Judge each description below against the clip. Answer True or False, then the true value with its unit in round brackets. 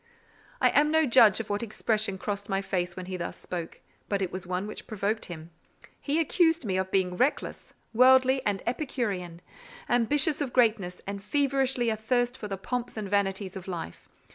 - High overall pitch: True (210 Hz)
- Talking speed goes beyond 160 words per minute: True (180 wpm)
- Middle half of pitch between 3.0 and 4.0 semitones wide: False (5.0 semitones)